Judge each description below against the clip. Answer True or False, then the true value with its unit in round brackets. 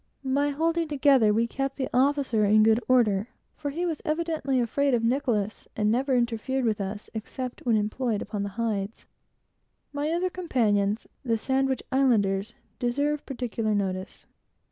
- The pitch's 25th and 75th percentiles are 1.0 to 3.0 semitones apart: False (4.6 semitones)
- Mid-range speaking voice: False (245 Hz)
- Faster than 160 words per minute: False (150 wpm)